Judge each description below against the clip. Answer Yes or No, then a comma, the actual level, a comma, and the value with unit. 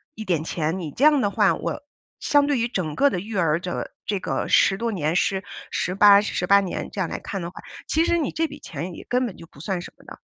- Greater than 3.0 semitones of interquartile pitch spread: Yes, wide, 5.4 semitones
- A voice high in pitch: Yes, high, 195 Hz